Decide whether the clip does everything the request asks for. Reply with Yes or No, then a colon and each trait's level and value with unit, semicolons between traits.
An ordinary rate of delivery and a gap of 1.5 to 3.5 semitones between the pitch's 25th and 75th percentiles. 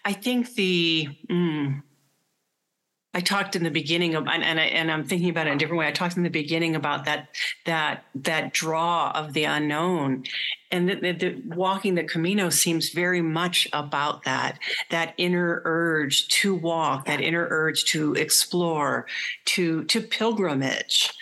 Yes: average, 170 wpm; narrow, 2.5 semitones